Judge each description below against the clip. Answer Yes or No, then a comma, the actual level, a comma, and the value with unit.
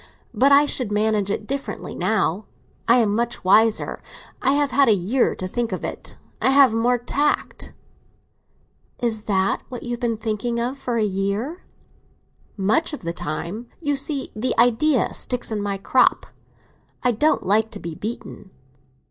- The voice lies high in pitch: Yes, high, 230 Hz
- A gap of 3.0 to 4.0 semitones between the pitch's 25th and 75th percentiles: Yes, average, 3.7 semitones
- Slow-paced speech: No, average, 165 wpm